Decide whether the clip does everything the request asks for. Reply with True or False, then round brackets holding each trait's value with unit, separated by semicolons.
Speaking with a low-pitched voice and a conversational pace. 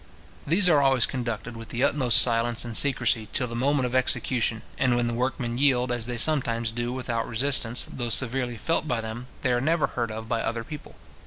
False (120 Hz; 210 wpm)